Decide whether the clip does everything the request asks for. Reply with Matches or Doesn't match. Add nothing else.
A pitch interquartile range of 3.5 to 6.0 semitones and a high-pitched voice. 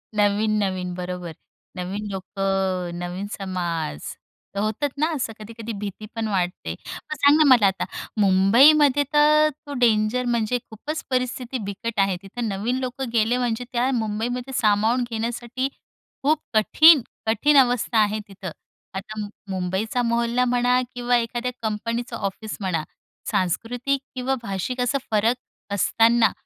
Matches